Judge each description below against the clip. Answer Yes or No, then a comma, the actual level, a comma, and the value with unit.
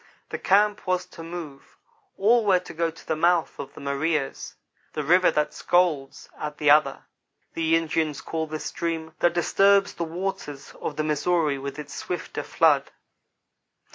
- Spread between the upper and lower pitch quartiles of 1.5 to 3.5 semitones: Yes, average, 2.8 semitones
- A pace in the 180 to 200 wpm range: No, average, 165 wpm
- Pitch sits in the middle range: Yes, medium, 160 Hz